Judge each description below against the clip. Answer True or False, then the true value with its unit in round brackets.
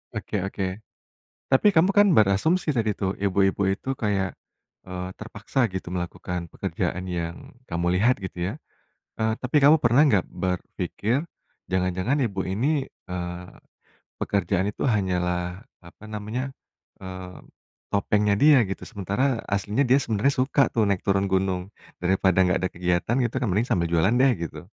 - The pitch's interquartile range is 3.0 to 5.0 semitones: True (4.5 semitones)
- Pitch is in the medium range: False (100 Hz)